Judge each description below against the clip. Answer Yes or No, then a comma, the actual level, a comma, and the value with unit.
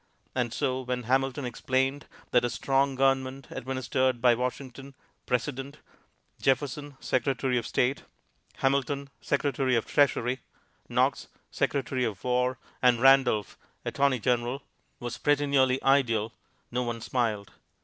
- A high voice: No, low, 130 Hz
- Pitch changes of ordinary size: No, narrow, 1.7 semitones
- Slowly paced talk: Yes, slow, 125 wpm